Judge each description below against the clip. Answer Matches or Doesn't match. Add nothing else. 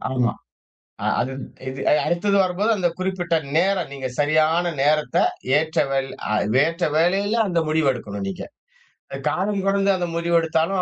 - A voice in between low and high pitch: Matches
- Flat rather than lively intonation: Doesn't match